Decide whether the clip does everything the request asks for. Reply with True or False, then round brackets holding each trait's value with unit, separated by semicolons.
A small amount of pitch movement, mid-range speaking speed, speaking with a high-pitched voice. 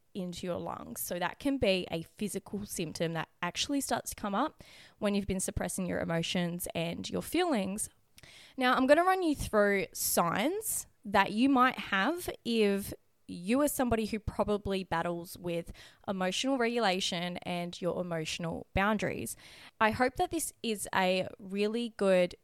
False (5.4 semitones; 160 wpm; 200 Hz)